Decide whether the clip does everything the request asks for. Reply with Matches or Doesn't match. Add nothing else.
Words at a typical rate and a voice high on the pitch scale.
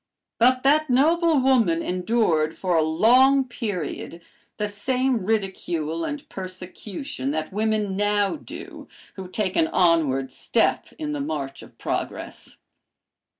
Doesn't match